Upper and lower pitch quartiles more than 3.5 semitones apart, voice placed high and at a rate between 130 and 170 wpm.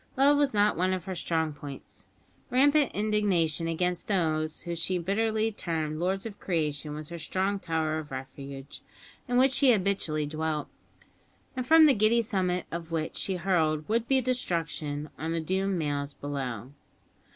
No: average, 5.3 semitones; medium, 170 Hz; average, 160 wpm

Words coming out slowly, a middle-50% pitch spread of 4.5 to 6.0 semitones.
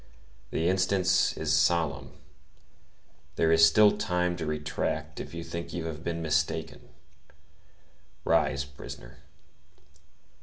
No: slow, 110 wpm; narrow, 2.4 semitones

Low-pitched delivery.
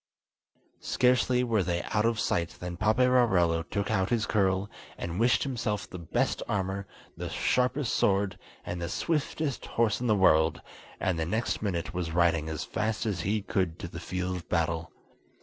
Yes: very low, 95 Hz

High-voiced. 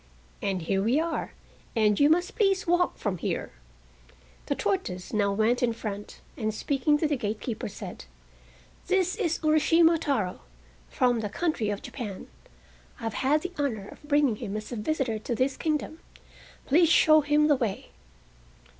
Yes: very high, 255 Hz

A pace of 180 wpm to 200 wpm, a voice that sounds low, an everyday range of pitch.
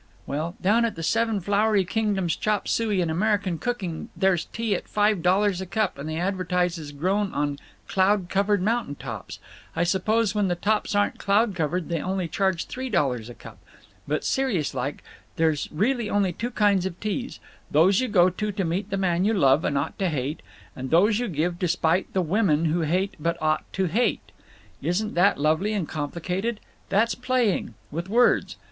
No: average, 185 wpm; high, 190 Hz; average, 4.1 semitones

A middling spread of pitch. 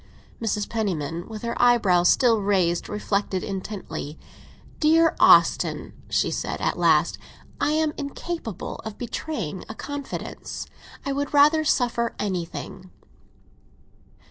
No: wide, 7.0 semitones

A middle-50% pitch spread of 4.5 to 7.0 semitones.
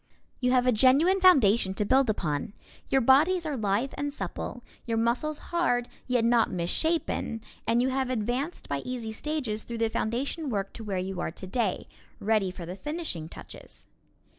Yes: average, 4.8 semitones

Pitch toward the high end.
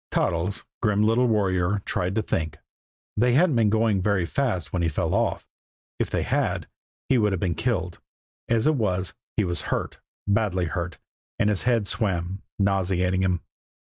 No: low, 100 Hz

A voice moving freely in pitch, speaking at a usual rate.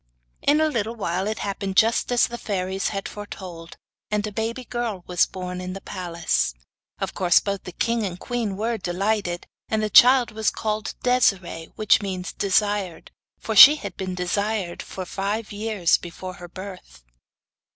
No: average, 3.3 semitones; average, 170 wpm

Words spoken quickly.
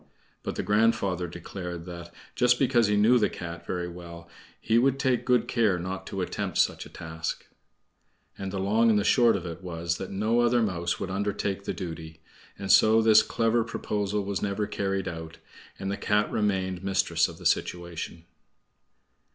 No: average, 180 wpm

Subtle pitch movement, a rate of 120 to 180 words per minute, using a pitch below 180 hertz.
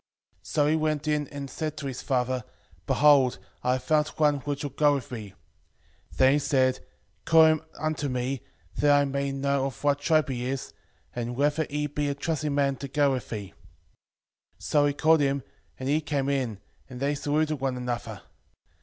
No: narrow, 2.3 semitones; average, 190 wpm; medium, 140 Hz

